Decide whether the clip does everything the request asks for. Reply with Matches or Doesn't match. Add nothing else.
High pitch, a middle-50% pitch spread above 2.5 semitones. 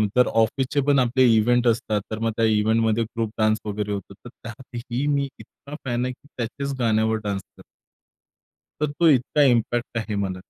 Doesn't match